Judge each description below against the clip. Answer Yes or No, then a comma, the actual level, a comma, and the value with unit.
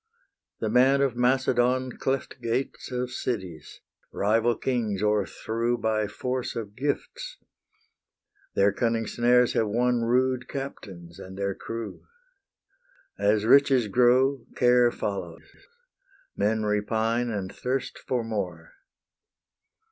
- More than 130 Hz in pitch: No, low, 120 Hz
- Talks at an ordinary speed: No, slow, 110 wpm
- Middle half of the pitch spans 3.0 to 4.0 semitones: Yes, average, 3.3 semitones